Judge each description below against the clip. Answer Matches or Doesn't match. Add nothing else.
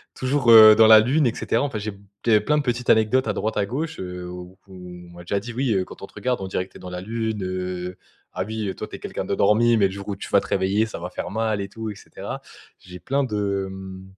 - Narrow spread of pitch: Doesn't match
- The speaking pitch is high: Doesn't match